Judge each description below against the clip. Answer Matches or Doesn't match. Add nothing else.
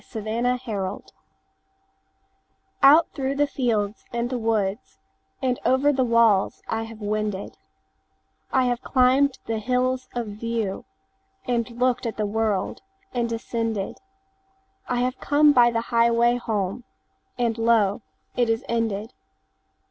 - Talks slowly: Matches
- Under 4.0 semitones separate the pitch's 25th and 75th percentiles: Matches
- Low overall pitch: Doesn't match